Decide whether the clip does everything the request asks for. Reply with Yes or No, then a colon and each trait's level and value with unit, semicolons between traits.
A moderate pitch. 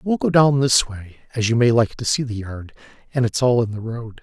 No: low, 120 Hz